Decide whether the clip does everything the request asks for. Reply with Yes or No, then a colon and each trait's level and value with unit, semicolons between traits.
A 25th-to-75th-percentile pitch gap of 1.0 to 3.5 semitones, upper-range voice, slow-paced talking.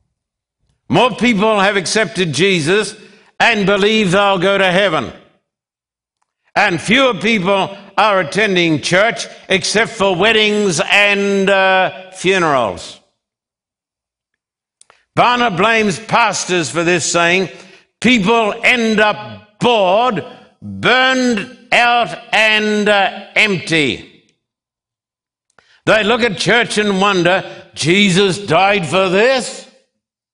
Yes: average, 2.8 semitones; high, 200 Hz; slow, 95 wpm